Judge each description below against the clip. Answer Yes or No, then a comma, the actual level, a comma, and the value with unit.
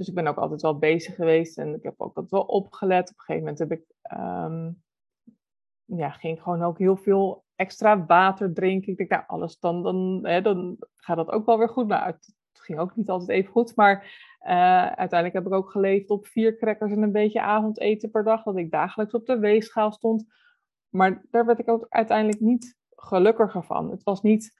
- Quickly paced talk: Yes, fast, 215 wpm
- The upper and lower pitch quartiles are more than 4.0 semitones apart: No, average, 3.7 semitones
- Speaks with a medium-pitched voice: No, high, 200 Hz